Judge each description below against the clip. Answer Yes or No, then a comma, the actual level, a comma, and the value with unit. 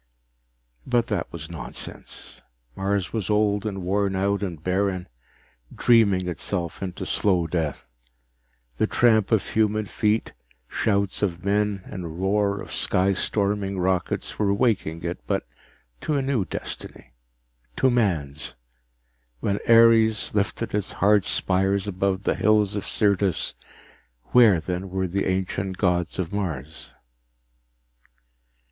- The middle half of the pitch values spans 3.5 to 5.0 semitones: No, narrow, 2.5 semitones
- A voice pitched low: Yes, low, 100 Hz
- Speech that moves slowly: Yes, slow, 125 wpm